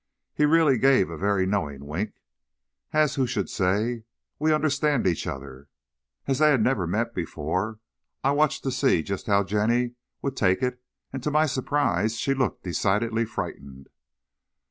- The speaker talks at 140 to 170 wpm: Yes, average, 160 wpm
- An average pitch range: No, wide, 6.5 semitones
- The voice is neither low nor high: No, low, 115 Hz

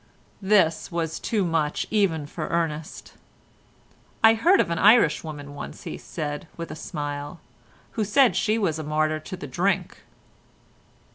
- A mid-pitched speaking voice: Yes, medium, 165 Hz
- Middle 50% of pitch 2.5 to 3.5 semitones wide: No, average, 4.7 semitones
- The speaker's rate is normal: Yes, average, 150 wpm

